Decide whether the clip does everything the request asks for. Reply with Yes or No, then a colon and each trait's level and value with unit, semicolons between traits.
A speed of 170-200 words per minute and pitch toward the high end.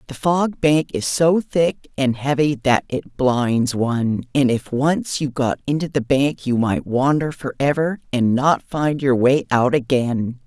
No: average, 180 wpm; low, 135 Hz